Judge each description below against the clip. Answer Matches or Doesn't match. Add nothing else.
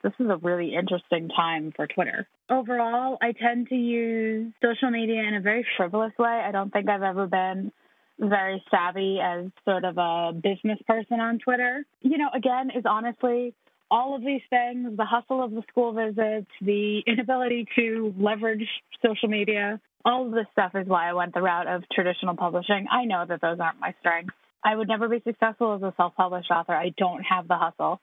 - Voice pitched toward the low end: Doesn't match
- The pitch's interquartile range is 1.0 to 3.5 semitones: Doesn't match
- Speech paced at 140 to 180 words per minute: Doesn't match